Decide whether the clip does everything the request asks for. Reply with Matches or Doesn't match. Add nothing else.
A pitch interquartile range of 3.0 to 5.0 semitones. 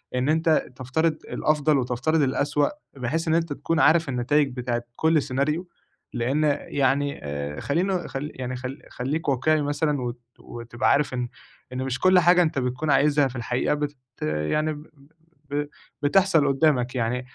Matches